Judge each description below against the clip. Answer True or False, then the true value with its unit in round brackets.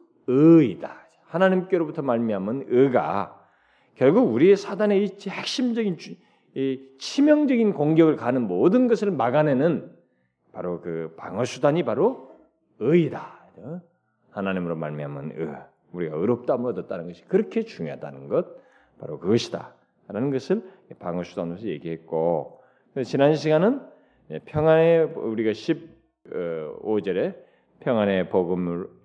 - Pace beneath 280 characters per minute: True (265 characters per minute)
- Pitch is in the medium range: True (155 Hz)